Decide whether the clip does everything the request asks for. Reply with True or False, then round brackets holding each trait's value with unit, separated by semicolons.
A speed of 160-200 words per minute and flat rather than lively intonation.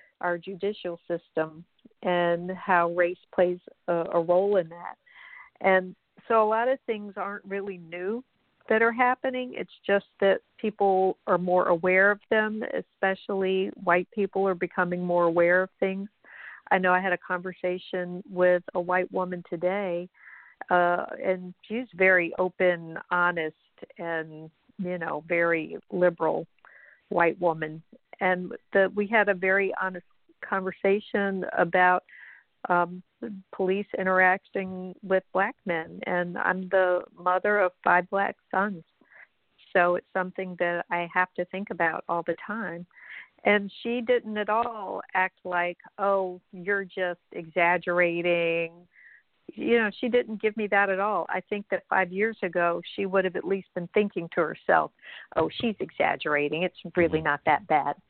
False (150 wpm; 2.1 semitones)